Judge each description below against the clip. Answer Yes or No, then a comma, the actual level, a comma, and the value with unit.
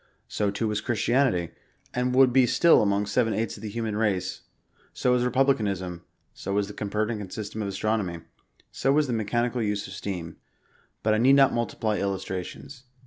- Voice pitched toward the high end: No, low, 110 Hz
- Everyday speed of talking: Yes, average, 185 wpm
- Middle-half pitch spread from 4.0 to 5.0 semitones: No, average, 3.6 semitones